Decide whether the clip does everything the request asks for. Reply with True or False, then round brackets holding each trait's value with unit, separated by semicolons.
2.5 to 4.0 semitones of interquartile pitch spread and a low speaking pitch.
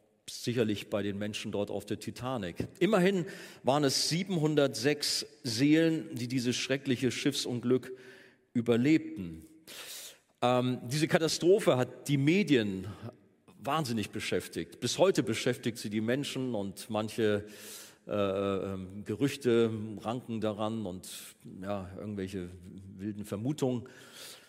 False (5.0 semitones; 120 Hz)